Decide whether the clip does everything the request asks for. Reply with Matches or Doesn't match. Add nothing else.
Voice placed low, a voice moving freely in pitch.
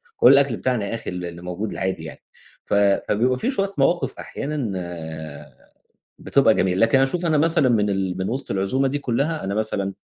Matches